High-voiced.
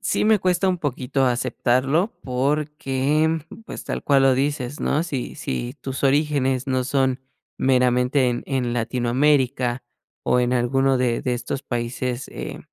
No: low, 130 Hz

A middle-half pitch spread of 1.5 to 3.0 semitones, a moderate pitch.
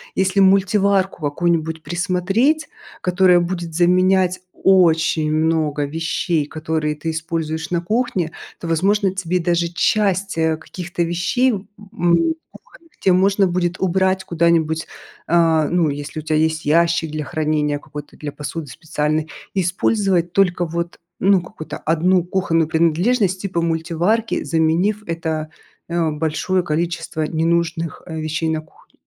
Yes: average, 2.7 semitones; medium, 170 Hz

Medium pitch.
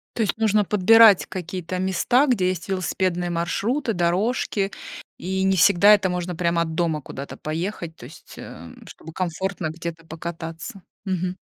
Yes: medium, 180 Hz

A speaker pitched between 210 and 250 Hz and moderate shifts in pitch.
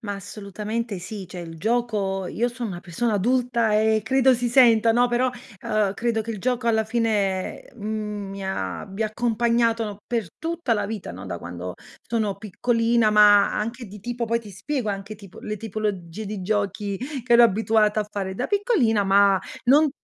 Yes: high, 215 Hz; average, 3.0 semitones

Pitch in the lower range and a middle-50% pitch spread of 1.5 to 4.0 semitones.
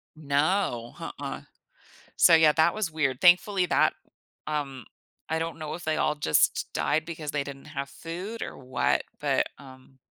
No: medium, 155 Hz; average, 3.1 semitones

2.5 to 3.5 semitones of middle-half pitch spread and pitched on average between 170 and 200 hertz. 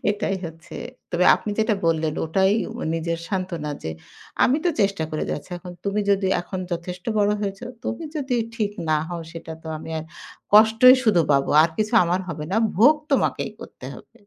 No: average, 4.3 semitones; medium, 185 Hz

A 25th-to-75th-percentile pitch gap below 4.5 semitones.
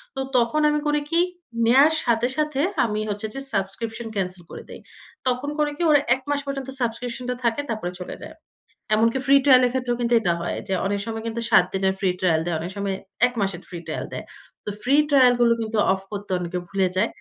No: average, 4.8 semitones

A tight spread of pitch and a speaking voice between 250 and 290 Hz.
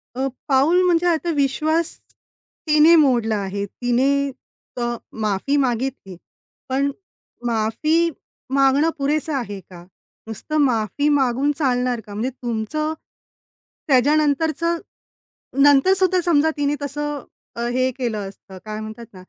No: average, 4.7 semitones; very high, 270 Hz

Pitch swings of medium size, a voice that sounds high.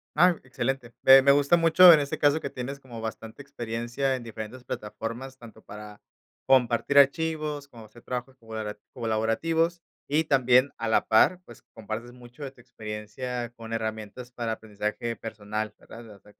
No: average, 3.8 semitones; low, 120 Hz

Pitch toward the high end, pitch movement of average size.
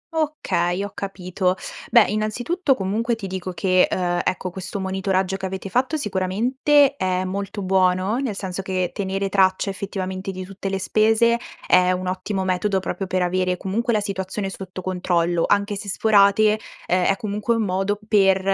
No: high, 195 Hz; narrow, 2.3 semitones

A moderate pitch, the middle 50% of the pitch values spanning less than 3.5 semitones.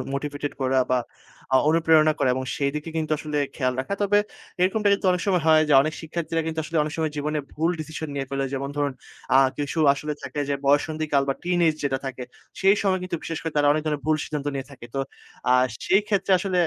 Yes: medium, 155 Hz; average, 2.8 semitones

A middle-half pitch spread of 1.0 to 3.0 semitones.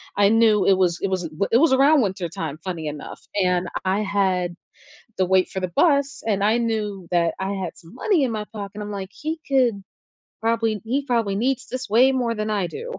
No: average, 4.3 semitones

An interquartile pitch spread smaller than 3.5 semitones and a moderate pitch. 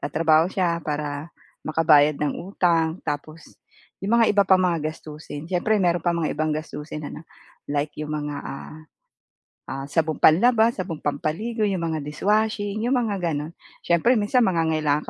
No: average, 4.3 semitones; medium, 165 Hz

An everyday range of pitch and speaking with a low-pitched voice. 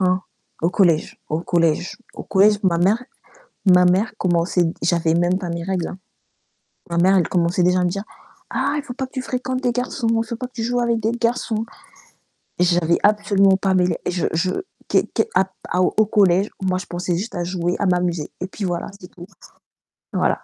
No: average, 3.4 semitones; medium, 185 Hz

